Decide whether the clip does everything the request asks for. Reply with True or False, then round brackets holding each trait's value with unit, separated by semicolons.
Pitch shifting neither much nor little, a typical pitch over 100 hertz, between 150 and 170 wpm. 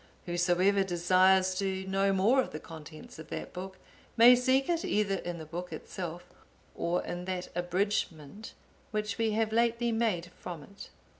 True (3.3 semitones; 190 Hz; 160 wpm)